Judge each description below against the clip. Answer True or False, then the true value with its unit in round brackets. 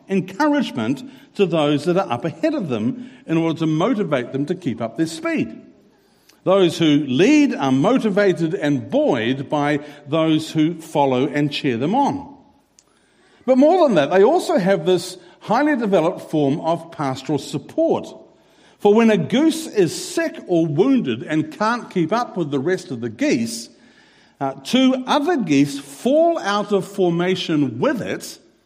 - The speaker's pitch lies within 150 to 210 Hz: True (185 Hz)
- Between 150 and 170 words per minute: True (160 wpm)